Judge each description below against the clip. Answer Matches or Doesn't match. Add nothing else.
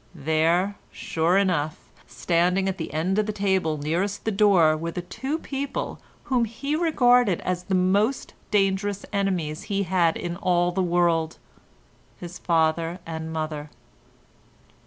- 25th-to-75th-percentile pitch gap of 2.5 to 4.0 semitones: Matches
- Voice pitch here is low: Doesn't match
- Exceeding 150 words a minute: Doesn't match